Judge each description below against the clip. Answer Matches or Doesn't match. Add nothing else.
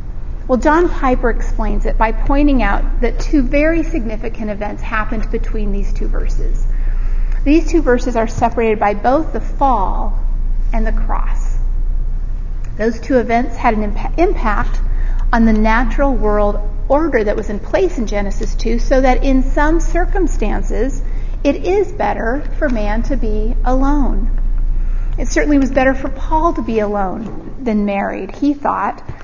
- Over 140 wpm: Matches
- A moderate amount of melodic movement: Matches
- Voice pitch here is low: Doesn't match